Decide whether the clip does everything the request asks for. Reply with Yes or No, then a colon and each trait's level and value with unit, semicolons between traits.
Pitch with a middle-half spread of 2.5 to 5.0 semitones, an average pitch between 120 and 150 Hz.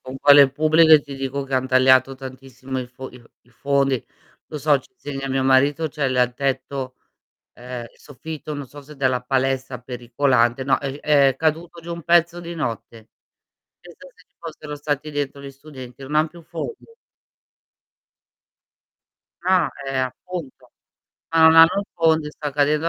Yes: average, 2.9 semitones; medium, 140 Hz